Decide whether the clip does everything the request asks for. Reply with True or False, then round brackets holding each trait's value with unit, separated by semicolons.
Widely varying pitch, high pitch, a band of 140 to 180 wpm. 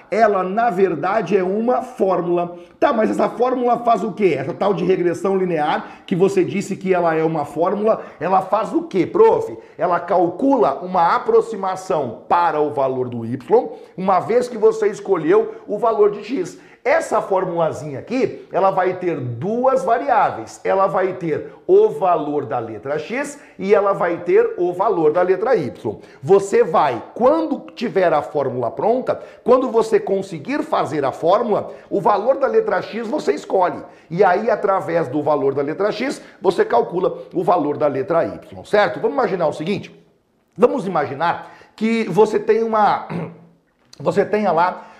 True (7.8 semitones; 205 Hz; 165 wpm)